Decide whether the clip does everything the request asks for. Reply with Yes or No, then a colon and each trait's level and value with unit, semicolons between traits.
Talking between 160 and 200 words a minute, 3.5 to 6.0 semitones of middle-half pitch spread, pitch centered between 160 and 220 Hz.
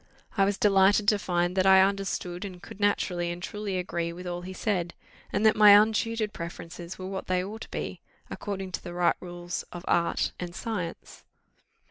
No: average, 190 wpm; narrow, 2.6 semitones; medium, 185 Hz